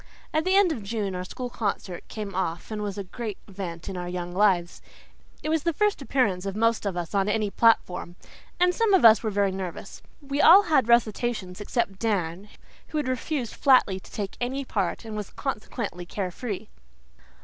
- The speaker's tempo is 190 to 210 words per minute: Yes, average, 195 wpm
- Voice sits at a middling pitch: No, high, 210 Hz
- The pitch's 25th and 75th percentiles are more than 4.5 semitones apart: Yes, average, 5.2 semitones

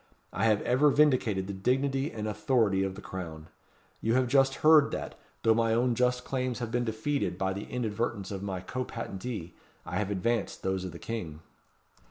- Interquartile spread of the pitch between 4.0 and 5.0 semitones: Yes, average, 4.7 semitones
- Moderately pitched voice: No, low, 115 Hz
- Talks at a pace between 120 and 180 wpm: No, average, 190 wpm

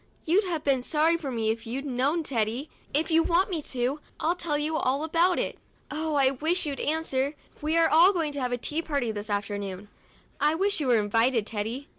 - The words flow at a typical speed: No, fast, 220 wpm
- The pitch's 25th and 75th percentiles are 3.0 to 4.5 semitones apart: No, average, 4.9 semitones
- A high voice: Yes, very high, 285 Hz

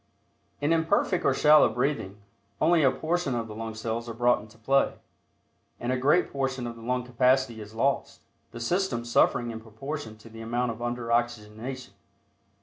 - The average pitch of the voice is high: No, low, 120 Hz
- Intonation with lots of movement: No, average, 3.3 semitones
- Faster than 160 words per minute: Yes, average, 175 wpm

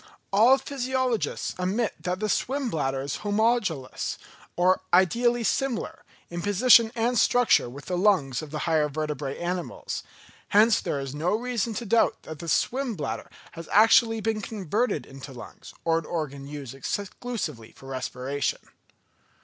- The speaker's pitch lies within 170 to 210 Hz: Yes, medium, 185 Hz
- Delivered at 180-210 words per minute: No, average, 150 wpm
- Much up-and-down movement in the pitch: Yes, wide, 7.6 semitones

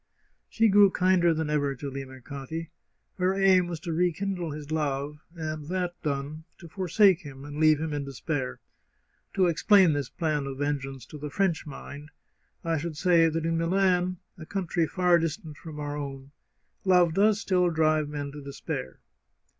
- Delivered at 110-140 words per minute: No, average, 170 wpm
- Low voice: No, medium, 160 Hz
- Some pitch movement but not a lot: Yes, average, 3.6 semitones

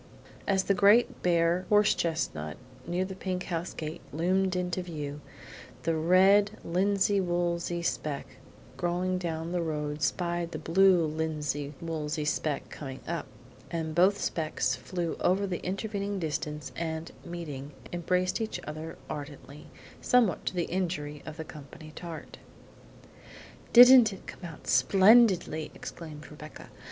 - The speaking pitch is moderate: Yes, medium, 170 Hz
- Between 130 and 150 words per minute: Yes, slow, 135 wpm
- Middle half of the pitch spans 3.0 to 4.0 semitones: Yes, average, 3.3 semitones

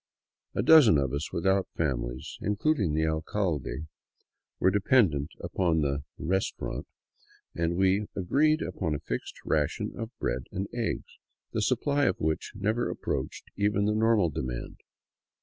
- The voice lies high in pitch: No, very low, 95 Hz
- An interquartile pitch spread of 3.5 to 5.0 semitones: No, wide, 5.5 semitones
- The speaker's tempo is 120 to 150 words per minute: Yes, average, 140 wpm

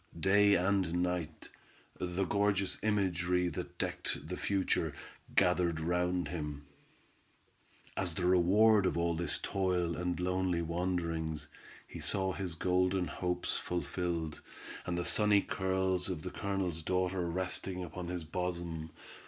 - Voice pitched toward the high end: No, very low, 90 Hz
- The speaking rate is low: Yes, slow, 130 wpm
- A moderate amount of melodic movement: No, narrow, 1.7 semitones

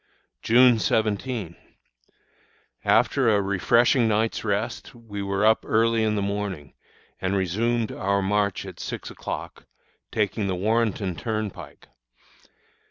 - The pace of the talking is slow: Yes, slow, 115 wpm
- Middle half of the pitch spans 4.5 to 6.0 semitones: No, narrow, 2.4 semitones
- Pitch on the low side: Yes, low, 105 Hz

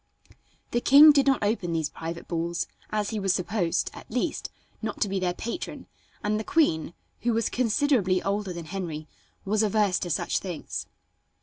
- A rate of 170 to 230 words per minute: Yes, average, 175 wpm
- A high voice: Yes, high, 200 Hz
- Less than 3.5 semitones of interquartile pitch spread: No, average, 4.7 semitones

